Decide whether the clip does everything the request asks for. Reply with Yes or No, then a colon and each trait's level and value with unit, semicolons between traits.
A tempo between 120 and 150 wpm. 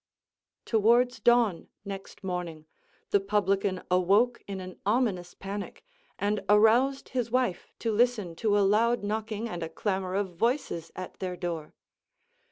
Yes: average, 140 wpm